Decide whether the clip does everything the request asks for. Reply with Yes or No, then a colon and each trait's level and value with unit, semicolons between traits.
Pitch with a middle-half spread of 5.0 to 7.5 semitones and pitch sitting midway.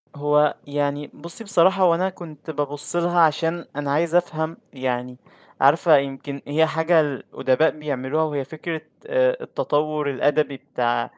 No: average, 2.8 semitones; medium, 150 Hz